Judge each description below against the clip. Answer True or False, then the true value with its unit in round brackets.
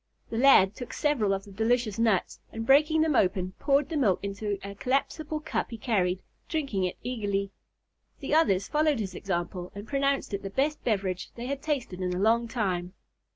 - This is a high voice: True (225 Hz)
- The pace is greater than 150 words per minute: True (190 wpm)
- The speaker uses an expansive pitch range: True (6.1 semitones)